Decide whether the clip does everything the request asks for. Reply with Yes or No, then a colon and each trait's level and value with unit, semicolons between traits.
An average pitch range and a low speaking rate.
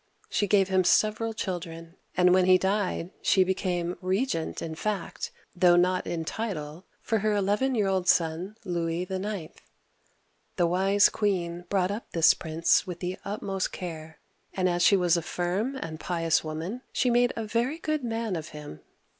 No: average, 3.4 semitones; average, 170 wpm